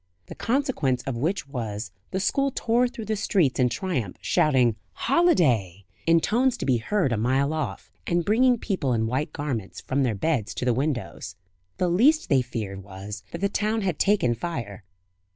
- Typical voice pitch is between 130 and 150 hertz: Yes, medium, 140 Hz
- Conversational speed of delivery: Yes, average, 180 wpm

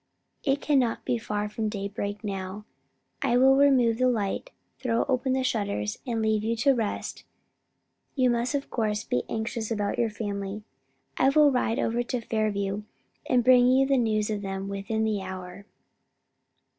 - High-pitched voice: Yes, high, 220 Hz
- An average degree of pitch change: Yes, average, 3.5 semitones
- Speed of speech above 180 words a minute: No, average, 165 wpm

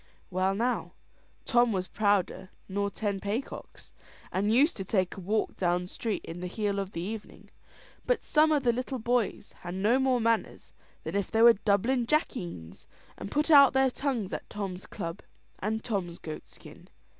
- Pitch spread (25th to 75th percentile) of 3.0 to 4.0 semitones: No, average, 4.5 semitones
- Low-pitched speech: No, high, 210 Hz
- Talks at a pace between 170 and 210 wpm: Yes, average, 175 wpm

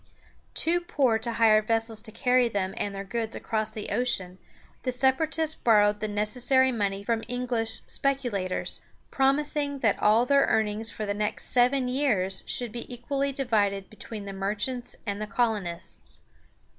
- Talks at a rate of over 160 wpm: No, average, 155 wpm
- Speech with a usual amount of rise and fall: Yes, average, 3.5 semitones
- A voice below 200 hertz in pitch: No, high, 225 Hz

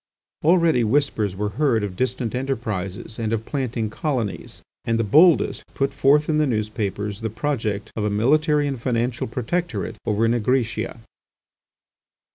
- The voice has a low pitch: Yes, low, 115 Hz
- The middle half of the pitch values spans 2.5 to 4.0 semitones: No, average, 4.6 semitones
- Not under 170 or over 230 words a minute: No, average, 140 wpm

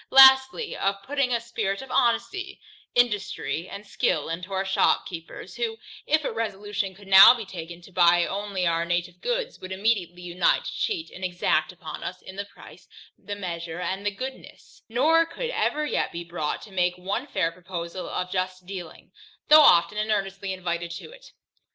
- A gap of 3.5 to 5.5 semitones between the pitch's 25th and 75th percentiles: Yes, average, 4.9 semitones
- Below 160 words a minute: No, average, 180 wpm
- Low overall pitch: No, high, 195 Hz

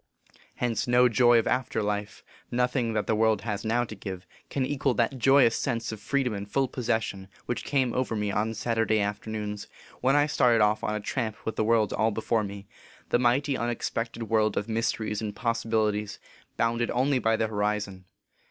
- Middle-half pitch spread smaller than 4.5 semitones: Yes, narrow, 2.4 semitones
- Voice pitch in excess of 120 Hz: No, low, 115 Hz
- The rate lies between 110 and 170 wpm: No, average, 190 wpm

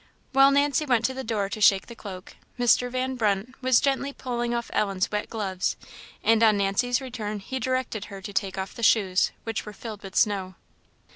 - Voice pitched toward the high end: Yes, high, 225 Hz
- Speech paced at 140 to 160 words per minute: No, average, 200 wpm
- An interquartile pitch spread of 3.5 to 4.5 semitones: Yes, average, 4.2 semitones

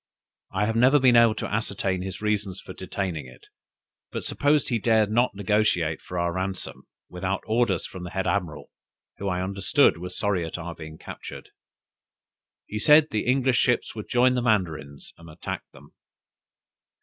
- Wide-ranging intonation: No, average, 4.2 semitones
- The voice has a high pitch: No, low, 100 Hz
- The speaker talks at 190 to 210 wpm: No, average, 170 wpm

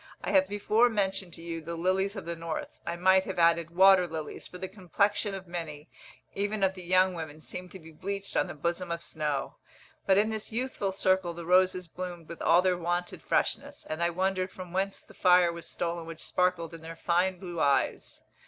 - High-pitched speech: No, medium, 180 Hz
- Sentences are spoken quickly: Yes, fast, 210 wpm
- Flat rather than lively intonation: Yes, narrow, 2.2 semitones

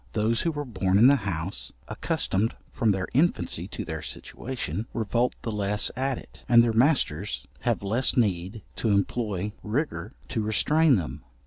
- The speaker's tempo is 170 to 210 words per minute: No, average, 160 wpm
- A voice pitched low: Yes, low, 110 Hz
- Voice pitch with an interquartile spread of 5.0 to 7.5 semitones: No, average, 4.0 semitones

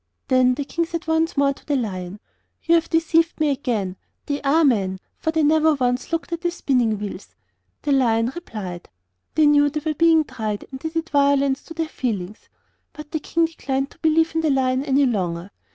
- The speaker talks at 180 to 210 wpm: Yes, average, 200 wpm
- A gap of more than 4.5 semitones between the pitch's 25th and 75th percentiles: Yes, average, 4.9 semitones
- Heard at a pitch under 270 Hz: No, very high, 280 Hz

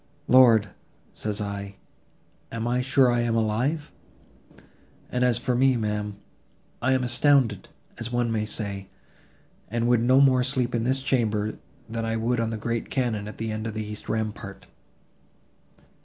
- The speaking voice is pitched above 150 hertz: No, low, 115 Hz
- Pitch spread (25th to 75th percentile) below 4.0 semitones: Yes, narrow, 2.6 semitones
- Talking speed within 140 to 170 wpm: Yes, average, 160 wpm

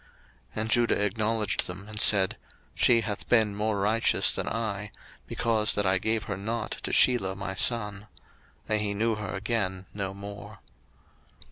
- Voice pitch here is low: Yes, low, 105 Hz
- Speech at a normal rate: Yes, average, 160 wpm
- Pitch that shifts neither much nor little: No, narrow, 2.0 semitones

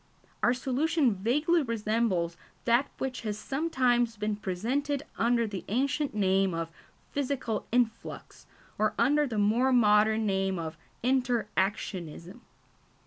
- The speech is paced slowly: Yes, slow, 120 wpm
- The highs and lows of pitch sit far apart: No, average, 4.2 semitones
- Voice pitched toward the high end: Yes, high, 230 Hz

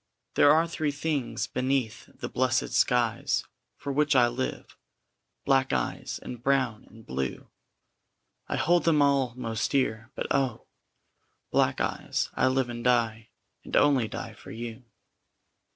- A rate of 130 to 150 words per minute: Yes, average, 140 wpm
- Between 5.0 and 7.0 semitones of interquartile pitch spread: No, average, 3.2 semitones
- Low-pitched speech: Yes, low, 125 Hz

